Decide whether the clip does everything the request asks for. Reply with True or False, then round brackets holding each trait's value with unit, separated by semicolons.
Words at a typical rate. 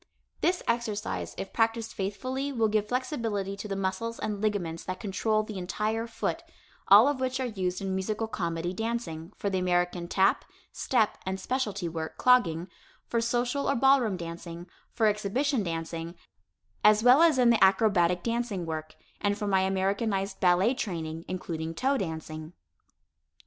True (155 wpm)